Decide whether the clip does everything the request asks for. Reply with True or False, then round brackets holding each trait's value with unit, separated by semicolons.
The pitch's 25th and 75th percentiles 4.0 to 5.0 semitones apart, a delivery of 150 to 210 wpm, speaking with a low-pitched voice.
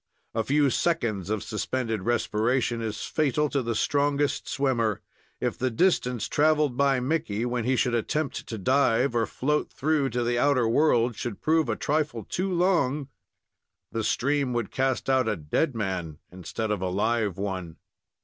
True (4.5 semitones; 165 wpm; 125 Hz)